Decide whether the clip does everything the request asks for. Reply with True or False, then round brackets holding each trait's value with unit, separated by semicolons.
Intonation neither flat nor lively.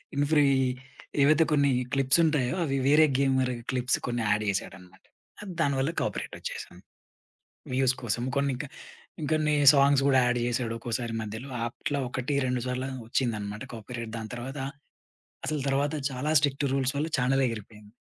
True (3.2 semitones)